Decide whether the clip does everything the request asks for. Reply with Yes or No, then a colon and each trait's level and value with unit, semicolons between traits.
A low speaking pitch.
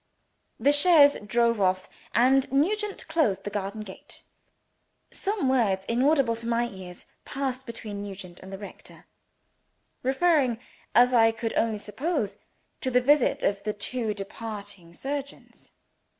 No: high, 230 Hz